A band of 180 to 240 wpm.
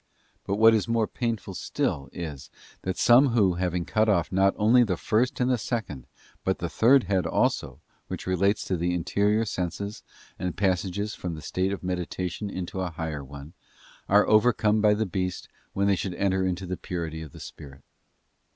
Yes: average, 185 wpm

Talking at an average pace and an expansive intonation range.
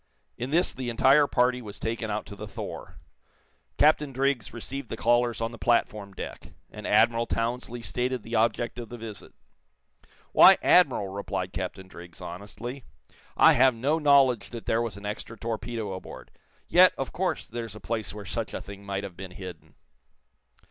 No: average, 175 wpm; average, 3.2 semitones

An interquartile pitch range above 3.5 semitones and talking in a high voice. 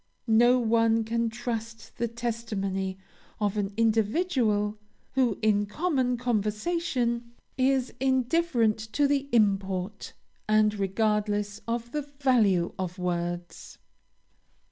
No: average, 3.2 semitones; high, 225 Hz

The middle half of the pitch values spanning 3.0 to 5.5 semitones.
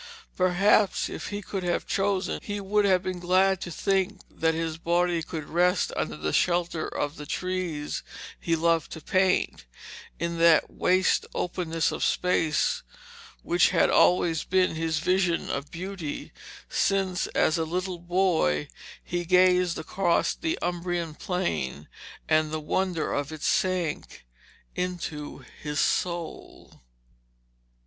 No: narrow, 2.4 semitones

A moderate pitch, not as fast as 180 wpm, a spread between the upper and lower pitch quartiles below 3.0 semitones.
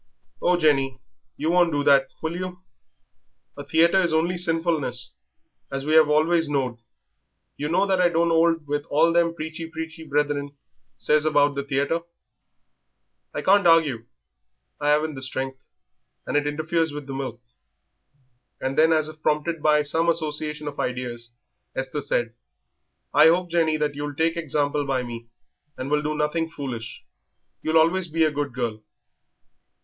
Yes: medium, 150 Hz; average, 160 wpm; narrow, 2.6 semitones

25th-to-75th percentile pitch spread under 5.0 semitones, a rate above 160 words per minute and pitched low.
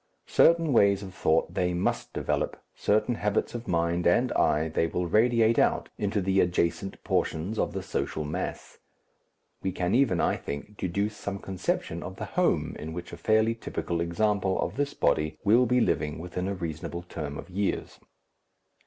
Yes: average, 4.2 semitones; average, 170 wpm; very low, 95 Hz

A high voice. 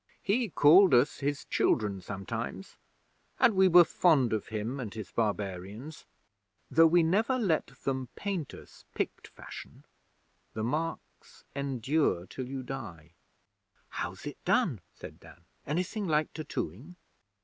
No: medium, 140 Hz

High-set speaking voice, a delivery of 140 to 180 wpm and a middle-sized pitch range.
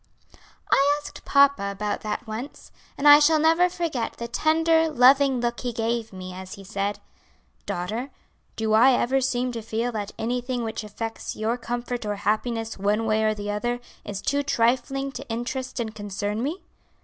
Yes: high, 235 Hz; average, 175 wpm; average, 3.9 semitones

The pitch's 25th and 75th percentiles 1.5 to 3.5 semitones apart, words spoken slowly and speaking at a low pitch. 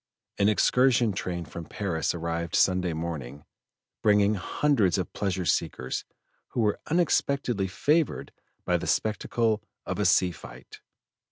No: average, 4.7 semitones; slow, 125 wpm; very low, 95 Hz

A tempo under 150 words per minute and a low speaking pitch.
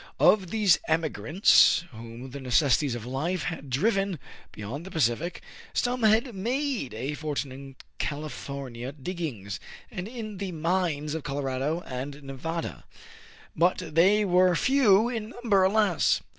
No: average, 140 wpm; medium, 160 Hz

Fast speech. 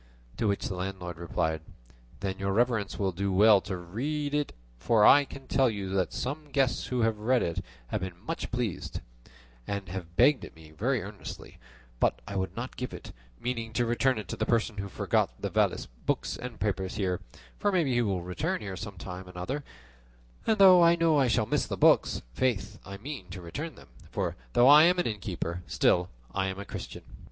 Yes: fast, 215 wpm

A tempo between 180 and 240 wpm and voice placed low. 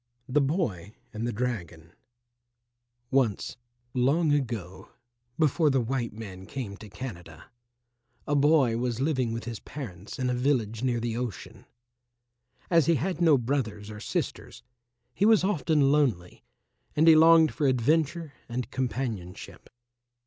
No: slow, 135 wpm; low, 125 Hz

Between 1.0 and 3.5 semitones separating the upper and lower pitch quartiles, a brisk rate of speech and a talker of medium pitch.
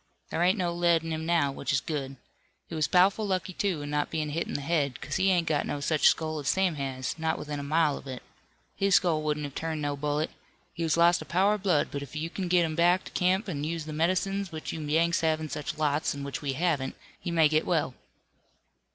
Yes: average, 2.9 semitones; fast, 255 wpm; medium, 160 Hz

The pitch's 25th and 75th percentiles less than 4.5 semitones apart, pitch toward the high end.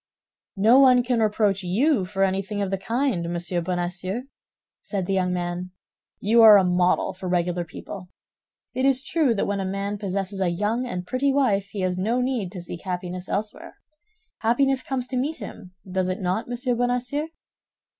No: average, 5.1 semitones; high, 200 Hz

